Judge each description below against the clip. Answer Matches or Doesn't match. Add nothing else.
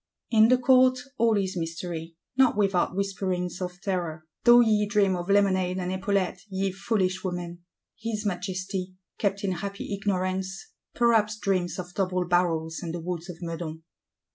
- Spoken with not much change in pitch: Matches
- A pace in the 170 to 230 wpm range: Doesn't match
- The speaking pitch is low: Doesn't match